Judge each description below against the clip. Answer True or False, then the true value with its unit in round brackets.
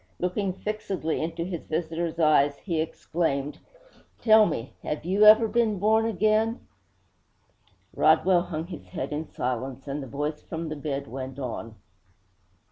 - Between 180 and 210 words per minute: False (135 wpm)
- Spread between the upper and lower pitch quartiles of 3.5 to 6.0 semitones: True (5.0 semitones)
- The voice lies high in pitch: False (160 Hz)